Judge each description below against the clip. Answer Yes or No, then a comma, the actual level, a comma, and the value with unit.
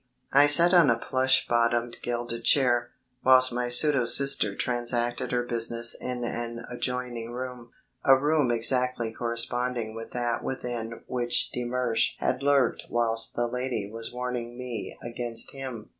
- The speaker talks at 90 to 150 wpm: Yes, average, 145 wpm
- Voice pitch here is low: Yes, low, 120 Hz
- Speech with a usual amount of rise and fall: No, narrow, 1.4 semitones